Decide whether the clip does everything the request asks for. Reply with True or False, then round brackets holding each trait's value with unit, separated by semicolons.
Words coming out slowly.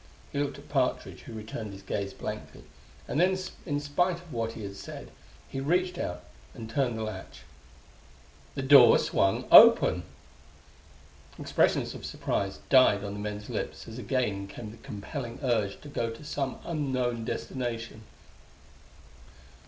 False (150 wpm)